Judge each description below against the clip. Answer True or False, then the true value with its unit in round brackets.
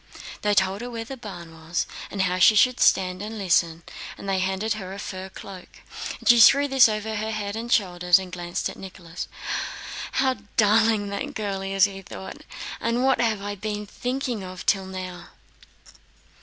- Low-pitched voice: False (200 Hz)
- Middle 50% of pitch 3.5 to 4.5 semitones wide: False (3.0 semitones)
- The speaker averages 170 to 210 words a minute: True (185 wpm)